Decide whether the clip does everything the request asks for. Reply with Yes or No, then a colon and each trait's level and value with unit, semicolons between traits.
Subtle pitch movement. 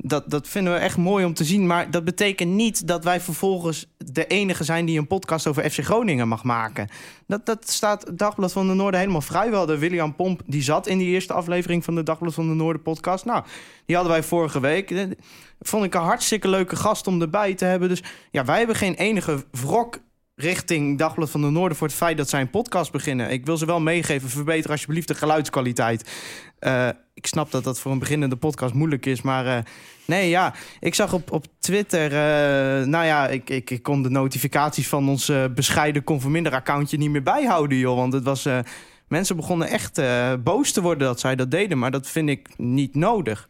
No: average, 4.5 semitones